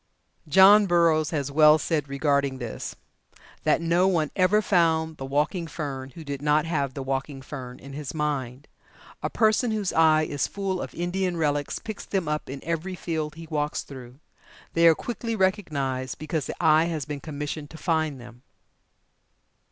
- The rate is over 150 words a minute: Yes, average, 175 wpm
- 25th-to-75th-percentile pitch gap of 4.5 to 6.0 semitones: No, average, 3.3 semitones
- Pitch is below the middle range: No, medium, 155 Hz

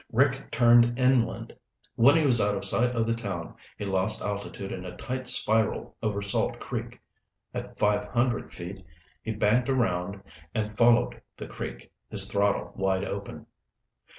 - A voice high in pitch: No, low, 110 Hz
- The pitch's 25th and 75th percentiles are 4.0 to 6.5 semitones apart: No, average, 3.2 semitones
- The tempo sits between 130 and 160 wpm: Yes, average, 155 wpm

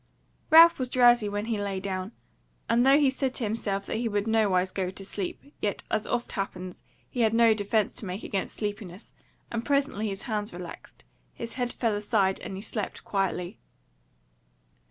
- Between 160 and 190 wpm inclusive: Yes, average, 180 wpm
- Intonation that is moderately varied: Yes, average, 3.2 semitones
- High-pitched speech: Yes, high, 210 Hz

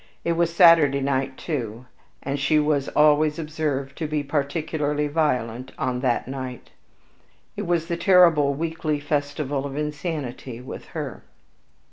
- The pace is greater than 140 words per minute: No, slow, 135 wpm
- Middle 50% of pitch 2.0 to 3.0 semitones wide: Yes, narrow, 2.6 semitones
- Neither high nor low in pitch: Yes, medium, 145 Hz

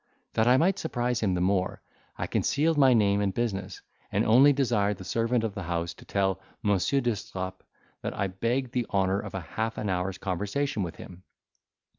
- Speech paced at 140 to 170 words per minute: No, average, 185 wpm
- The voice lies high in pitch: No, low, 105 Hz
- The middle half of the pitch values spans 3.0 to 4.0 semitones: No, average, 4.4 semitones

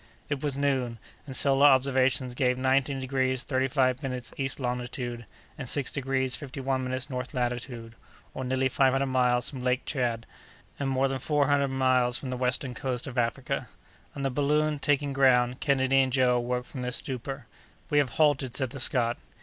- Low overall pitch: Yes, low, 130 Hz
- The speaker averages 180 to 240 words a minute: Yes, average, 185 wpm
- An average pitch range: No, narrow, 1.6 semitones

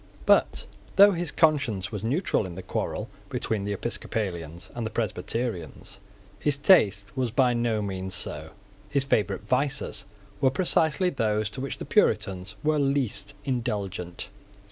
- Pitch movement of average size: No, wide, 5.9 semitones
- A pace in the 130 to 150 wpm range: Yes, average, 145 wpm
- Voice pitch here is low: Yes, low, 115 Hz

